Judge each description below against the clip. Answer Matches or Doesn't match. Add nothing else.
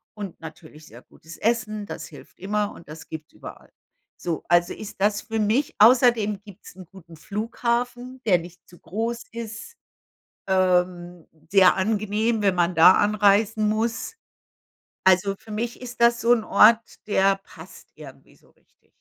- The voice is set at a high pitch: Matches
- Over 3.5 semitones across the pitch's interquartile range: Matches